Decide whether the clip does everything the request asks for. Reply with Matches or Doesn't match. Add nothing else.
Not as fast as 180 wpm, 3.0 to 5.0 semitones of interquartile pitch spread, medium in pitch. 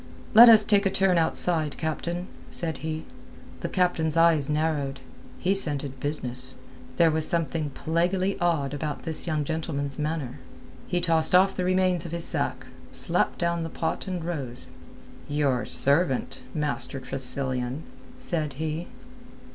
Matches